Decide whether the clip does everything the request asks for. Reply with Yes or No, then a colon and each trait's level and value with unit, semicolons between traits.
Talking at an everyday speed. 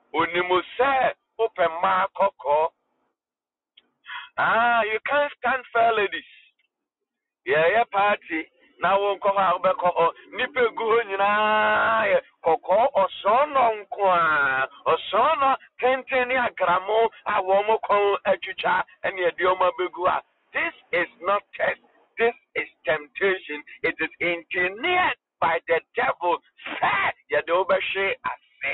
No: slow, 110 wpm